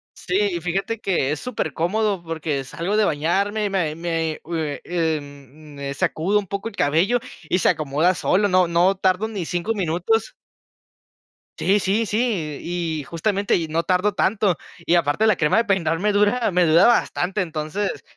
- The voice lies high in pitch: No, medium, 180 Hz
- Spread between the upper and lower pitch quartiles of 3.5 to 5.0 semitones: Yes, average, 4.3 semitones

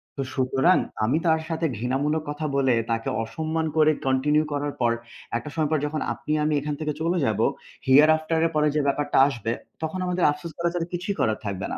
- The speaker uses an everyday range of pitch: Yes, average, 3.1 semitones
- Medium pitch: Yes, medium, 150 Hz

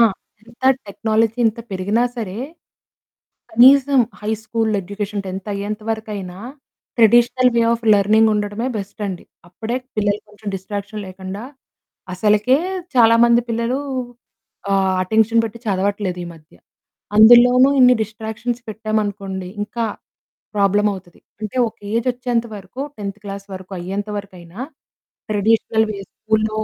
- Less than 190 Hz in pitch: No, high, 215 Hz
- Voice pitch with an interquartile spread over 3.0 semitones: No, narrow, 2.4 semitones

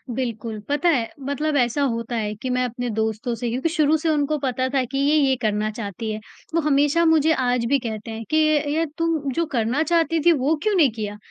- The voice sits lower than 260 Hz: No, very high, 265 Hz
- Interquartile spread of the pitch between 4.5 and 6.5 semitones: Yes, average, 5.0 semitones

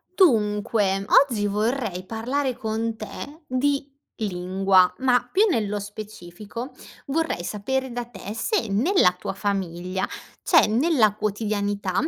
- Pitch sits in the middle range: No, high, 215 Hz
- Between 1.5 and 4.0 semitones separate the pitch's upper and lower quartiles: No, average, 4.4 semitones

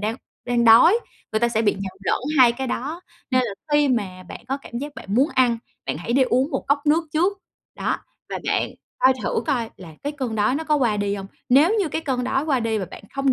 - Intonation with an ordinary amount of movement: Yes, average, 4.5 semitones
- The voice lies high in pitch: Yes, very high, 255 Hz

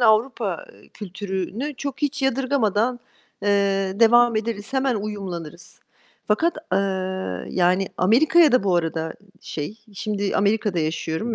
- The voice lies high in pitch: Yes, high, 215 Hz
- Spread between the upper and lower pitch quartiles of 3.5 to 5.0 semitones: Yes, average, 4.7 semitones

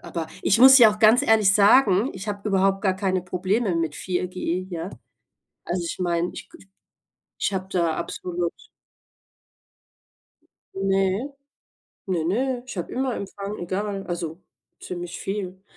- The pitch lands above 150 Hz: Yes, high, 190 Hz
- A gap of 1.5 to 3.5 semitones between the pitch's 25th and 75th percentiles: Yes, average, 2.7 semitones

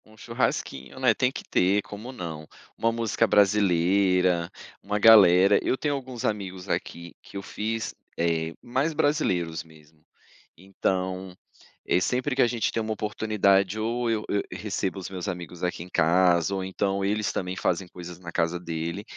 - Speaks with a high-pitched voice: No, very low, 95 Hz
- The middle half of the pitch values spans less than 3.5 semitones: No, average, 3.9 semitones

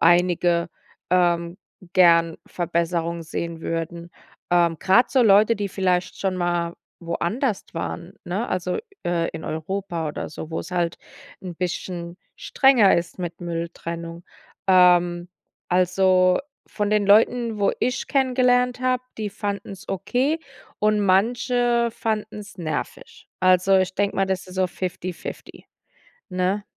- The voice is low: No, medium, 185 Hz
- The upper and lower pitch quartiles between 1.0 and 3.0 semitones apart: No, average, 3.4 semitones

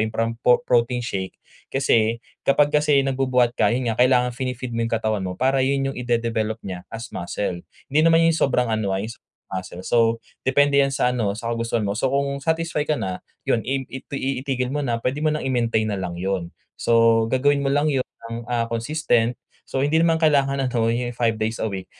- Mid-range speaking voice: No, low, 125 Hz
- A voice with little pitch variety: No, average, 3.3 semitones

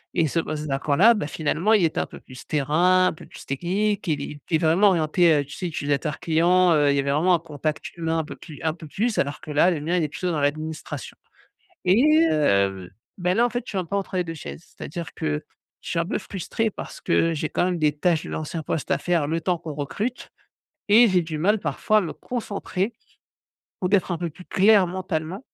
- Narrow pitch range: No, average, 3.4 semitones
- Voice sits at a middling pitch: Yes, medium, 165 Hz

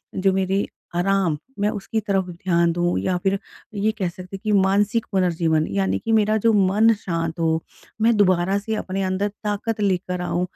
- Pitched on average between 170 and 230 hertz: Yes, high, 190 Hz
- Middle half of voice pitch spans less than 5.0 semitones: Yes, average, 2.8 semitones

